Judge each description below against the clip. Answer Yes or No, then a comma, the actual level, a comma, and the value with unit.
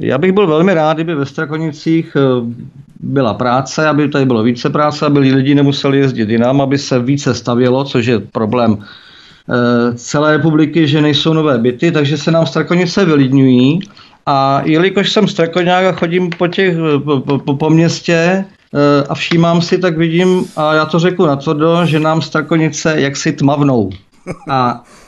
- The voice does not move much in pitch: No, average, 3.5 semitones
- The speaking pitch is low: No, medium, 150 Hz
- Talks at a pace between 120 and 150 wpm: No, average, 160 wpm